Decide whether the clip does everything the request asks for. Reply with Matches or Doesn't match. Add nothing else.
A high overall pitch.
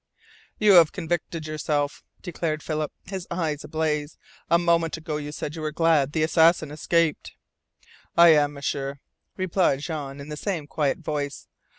Doesn't match